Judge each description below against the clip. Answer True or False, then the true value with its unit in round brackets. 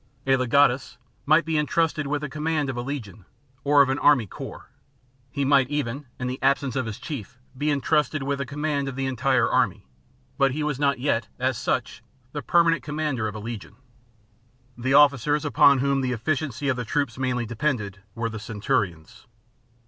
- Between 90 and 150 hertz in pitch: True (135 Hz)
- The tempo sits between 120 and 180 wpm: False (190 wpm)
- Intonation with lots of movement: False (3.2 semitones)